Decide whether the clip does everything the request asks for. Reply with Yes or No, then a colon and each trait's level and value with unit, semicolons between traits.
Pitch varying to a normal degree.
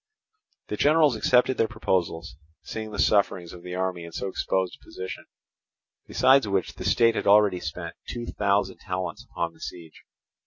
Yes: average, 3.7 semitones